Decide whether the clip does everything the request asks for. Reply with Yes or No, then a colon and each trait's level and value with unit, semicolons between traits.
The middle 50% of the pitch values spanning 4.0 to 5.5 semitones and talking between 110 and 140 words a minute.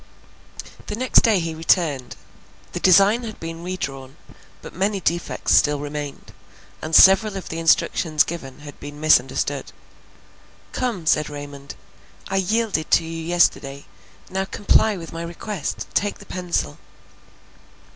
Yes: average, 4.7 semitones; slow, 135 wpm